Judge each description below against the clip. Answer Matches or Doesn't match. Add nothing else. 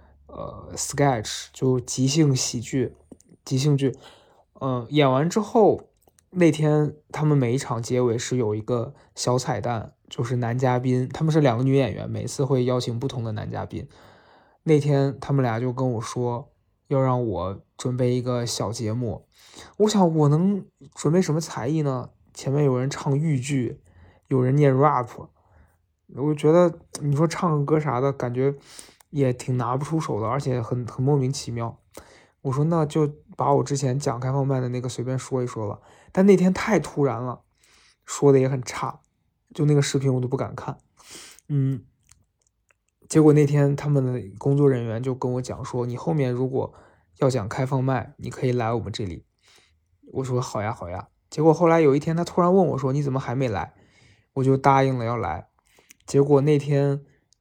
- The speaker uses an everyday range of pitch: Matches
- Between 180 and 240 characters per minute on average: Doesn't match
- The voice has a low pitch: Matches